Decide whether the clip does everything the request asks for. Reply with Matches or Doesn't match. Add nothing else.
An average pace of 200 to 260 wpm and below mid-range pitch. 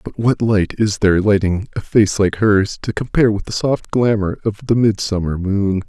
Matches